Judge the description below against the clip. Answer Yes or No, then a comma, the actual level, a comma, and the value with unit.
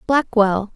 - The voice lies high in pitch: Yes, high, 220 Hz